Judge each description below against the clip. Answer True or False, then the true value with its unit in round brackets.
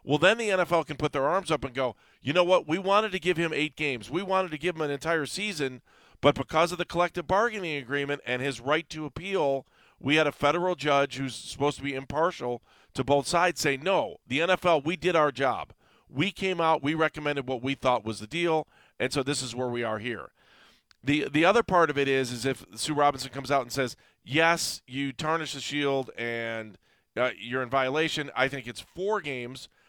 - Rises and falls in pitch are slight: False (3.8 semitones)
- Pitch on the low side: False (145 Hz)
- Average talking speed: False (225 wpm)